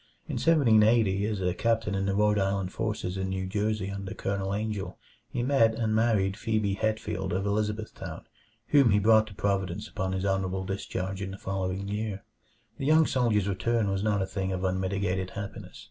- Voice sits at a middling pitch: No, low, 100 Hz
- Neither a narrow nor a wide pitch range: No, narrow, 2.3 semitones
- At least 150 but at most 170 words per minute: No, average, 180 wpm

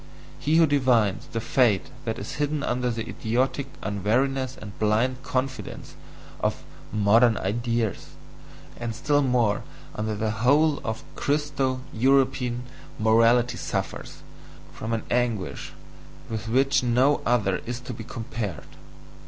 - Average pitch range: Yes, average, 3.1 semitones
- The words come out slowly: Yes, slow, 125 wpm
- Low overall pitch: Yes, low, 120 Hz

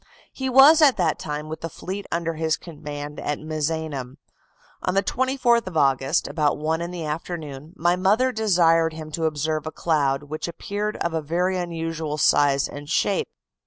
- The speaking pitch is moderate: Yes, medium, 160 Hz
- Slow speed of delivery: No, average, 175 wpm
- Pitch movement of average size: Yes, average, 3.4 semitones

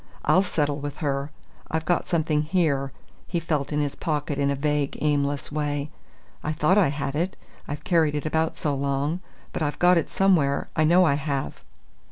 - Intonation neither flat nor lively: No, narrow, 2.3 semitones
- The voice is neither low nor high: Yes, medium, 150 Hz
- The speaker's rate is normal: Yes, average, 195 wpm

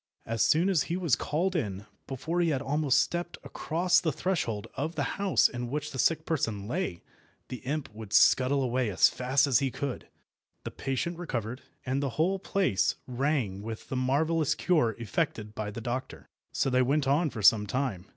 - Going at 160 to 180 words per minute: No, average, 190 wpm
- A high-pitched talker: No, low, 135 Hz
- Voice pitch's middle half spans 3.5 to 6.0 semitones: Yes, wide, 5.4 semitones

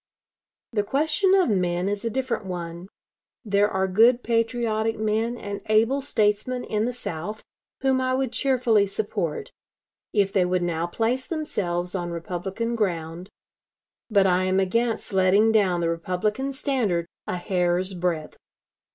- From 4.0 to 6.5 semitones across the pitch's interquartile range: Yes, average, 4.5 semitones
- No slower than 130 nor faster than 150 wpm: Yes, average, 145 wpm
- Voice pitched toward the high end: Yes, high, 205 Hz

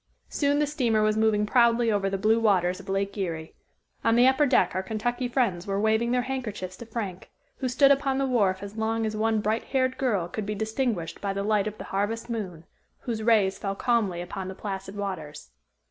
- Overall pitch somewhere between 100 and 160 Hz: No, high, 215 Hz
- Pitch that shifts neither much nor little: Yes, average, 3.5 semitones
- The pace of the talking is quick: Yes, fast, 210 wpm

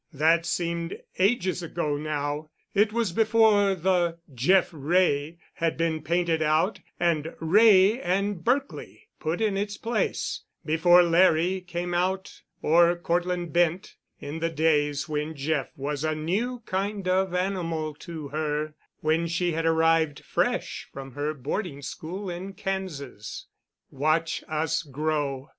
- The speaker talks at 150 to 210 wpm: No, slow, 135 wpm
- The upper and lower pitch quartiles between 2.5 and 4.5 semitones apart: Yes, average, 3.3 semitones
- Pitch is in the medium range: Yes, medium, 165 Hz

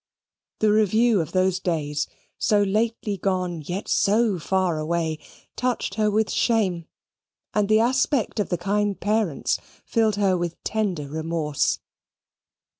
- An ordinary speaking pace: No, slow, 130 wpm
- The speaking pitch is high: Yes, high, 195 Hz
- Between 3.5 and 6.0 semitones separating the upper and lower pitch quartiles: Yes, average, 4.0 semitones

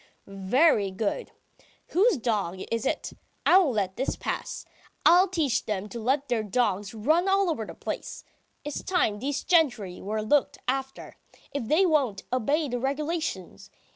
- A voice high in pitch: Yes, very high, 255 Hz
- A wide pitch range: Yes, wide, 6.9 semitones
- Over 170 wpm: No, average, 155 wpm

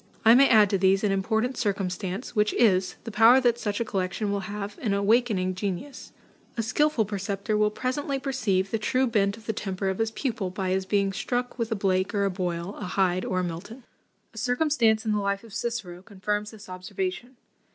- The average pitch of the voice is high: Yes, high, 210 Hz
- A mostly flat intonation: No, average, 3.3 semitones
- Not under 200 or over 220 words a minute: Yes, fast, 205 wpm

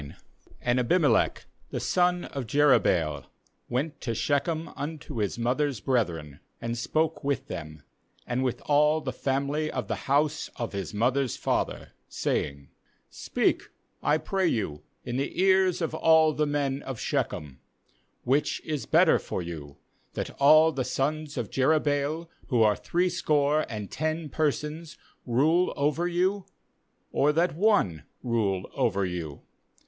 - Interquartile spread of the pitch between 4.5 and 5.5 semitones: Yes, average, 5.2 semitones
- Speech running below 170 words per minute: Yes, average, 145 wpm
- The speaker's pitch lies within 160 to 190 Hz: No, medium, 140 Hz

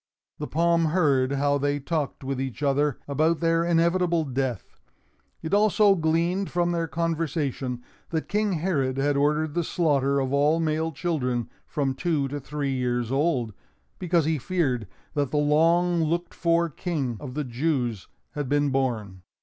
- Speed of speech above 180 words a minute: No, average, 160 wpm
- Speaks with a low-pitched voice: No, medium, 150 Hz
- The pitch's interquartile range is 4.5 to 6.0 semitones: No, average, 3.7 semitones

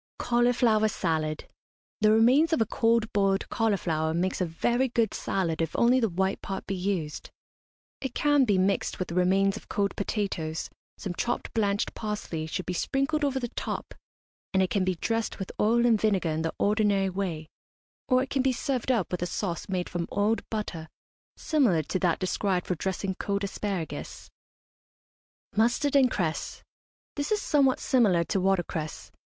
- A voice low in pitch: No, high, 200 Hz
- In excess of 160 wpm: Yes, average, 170 wpm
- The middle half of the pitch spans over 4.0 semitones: Yes, average, 4.7 semitones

